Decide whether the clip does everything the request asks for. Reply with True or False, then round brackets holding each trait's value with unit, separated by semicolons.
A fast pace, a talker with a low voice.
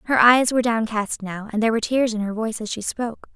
False (270 wpm; 225 Hz)